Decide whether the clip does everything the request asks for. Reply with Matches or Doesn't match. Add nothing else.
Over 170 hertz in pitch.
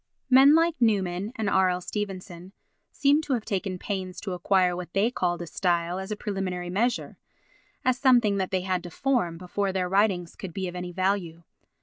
Matches